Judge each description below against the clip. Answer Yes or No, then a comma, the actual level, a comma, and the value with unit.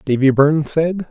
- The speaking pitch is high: No, medium, 150 Hz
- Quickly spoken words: No, average, 165 wpm